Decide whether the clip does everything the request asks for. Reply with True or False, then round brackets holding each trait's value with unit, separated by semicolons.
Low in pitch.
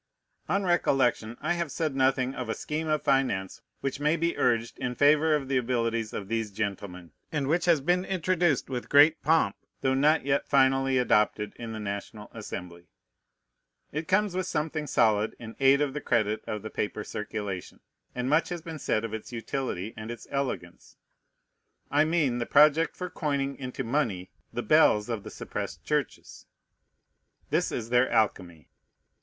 True (130 Hz)